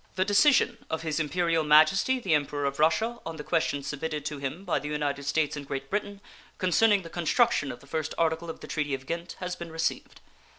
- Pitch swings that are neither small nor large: Yes, average, 3.5 semitones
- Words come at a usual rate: No, fast, 215 wpm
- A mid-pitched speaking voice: Yes, medium, 160 Hz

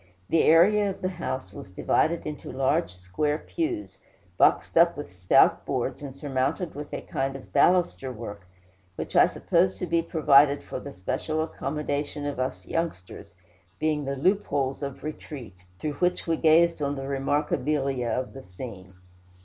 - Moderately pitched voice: Yes, medium, 145 Hz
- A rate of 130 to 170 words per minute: Yes, average, 160 wpm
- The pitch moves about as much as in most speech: Yes, average, 3.9 semitones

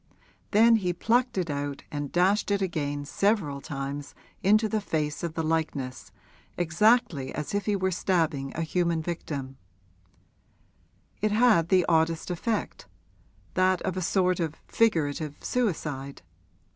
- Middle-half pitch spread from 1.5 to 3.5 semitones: No, average, 5.2 semitones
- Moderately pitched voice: Yes, medium, 170 Hz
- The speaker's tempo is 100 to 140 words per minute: Yes, slow, 135 wpm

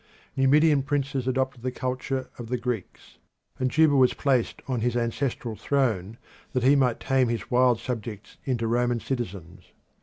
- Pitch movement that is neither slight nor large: No, narrow, 2.3 semitones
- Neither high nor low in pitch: No, low, 125 Hz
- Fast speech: No, average, 155 wpm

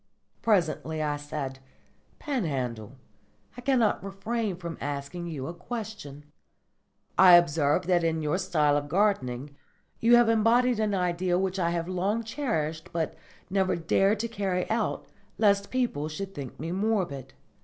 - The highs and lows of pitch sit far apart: Yes, wide, 5.7 semitones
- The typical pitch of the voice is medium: Yes, medium, 180 Hz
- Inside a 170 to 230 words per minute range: No, average, 145 wpm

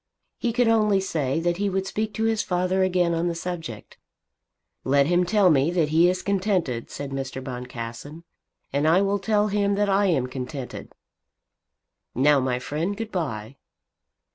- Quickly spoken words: No, average, 165 wpm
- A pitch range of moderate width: No, wide, 6.3 semitones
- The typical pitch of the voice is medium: Yes, medium, 175 Hz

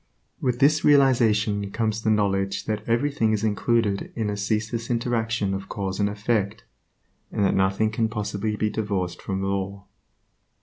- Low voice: Yes, low, 105 Hz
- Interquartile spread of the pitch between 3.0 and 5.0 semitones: No, narrow, 2.4 semitones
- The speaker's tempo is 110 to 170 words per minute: Yes, average, 150 wpm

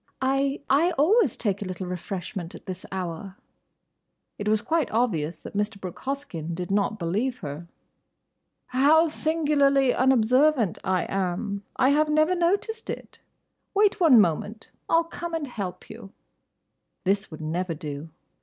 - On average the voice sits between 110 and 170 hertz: No, high, 220 Hz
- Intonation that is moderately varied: No, wide, 8.1 semitones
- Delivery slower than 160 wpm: Yes, average, 145 wpm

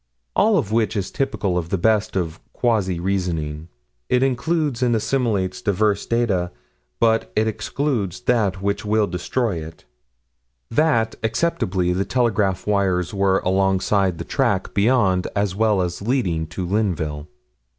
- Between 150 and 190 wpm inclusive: No, average, 140 wpm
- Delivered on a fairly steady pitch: No, average, 3.9 semitones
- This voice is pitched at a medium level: No, low, 100 Hz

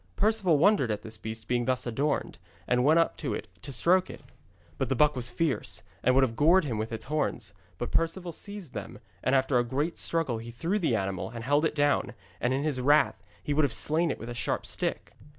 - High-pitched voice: No, low, 135 Hz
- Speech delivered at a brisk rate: Yes, fast, 230 wpm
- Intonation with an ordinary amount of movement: Yes, average, 5.0 semitones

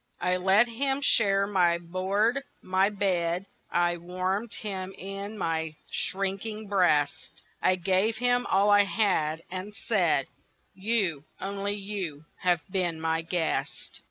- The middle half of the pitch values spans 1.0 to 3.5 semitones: Yes, average, 2.8 semitones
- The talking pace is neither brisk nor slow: No, slow, 130 wpm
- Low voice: No, high, 190 Hz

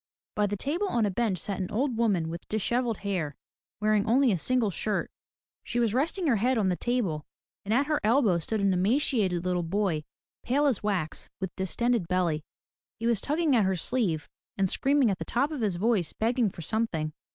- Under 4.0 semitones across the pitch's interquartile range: No, average, 5.0 semitones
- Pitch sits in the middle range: No, high, 215 Hz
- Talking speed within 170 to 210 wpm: Yes, average, 200 wpm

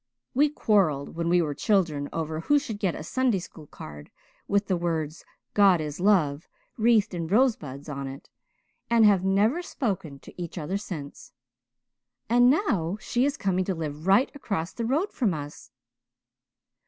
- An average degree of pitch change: No, wide, 6.1 semitones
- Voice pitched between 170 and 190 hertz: Yes, medium, 185 Hz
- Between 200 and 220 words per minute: No, average, 165 wpm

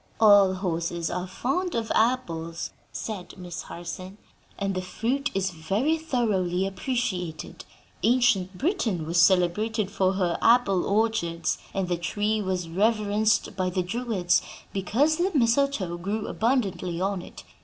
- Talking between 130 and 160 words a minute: Yes, slow, 135 wpm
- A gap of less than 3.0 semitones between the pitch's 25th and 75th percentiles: No, average, 4.2 semitones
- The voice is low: No, high, 195 Hz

